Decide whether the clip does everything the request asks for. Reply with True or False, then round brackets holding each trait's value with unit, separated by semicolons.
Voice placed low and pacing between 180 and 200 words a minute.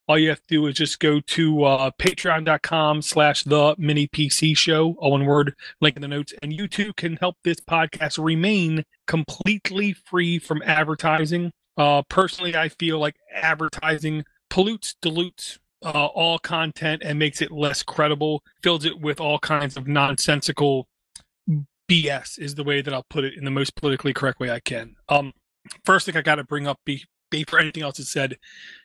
False (155 Hz; 185 wpm)